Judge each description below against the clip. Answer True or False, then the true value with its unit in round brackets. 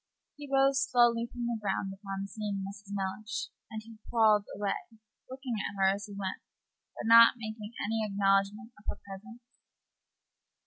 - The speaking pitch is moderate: False (210 Hz)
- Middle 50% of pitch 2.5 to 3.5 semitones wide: True (2.9 semitones)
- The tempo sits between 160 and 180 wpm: False (150 wpm)